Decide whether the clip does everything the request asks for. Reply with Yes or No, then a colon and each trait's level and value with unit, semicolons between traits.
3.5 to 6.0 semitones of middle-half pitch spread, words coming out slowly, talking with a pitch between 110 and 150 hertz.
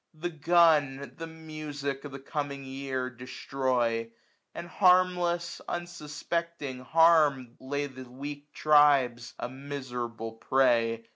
Yes: average, 3.8 semitones; slow, 110 wpm; medium, 140 Hz